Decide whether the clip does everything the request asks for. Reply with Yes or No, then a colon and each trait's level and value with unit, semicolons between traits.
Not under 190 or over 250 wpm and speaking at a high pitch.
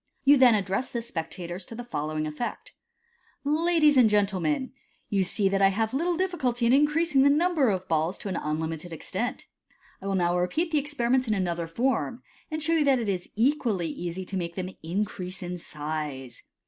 Yes: fast, 205 wpm; high, 210 Hz